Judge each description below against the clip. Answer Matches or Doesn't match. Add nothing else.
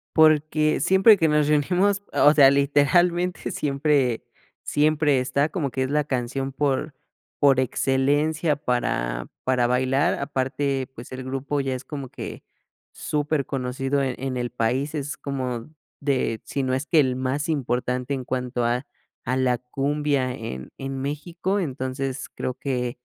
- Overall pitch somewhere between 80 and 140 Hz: Matches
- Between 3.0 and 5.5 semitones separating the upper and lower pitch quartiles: Doesn't match